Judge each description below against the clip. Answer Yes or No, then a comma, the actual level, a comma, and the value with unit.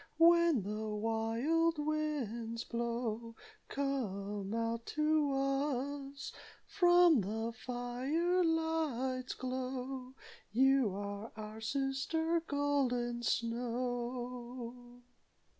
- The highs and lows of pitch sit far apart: No, average, 3.8 semitones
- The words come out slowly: Yes, slow, 75 wpm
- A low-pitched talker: No, very high, 250 Hz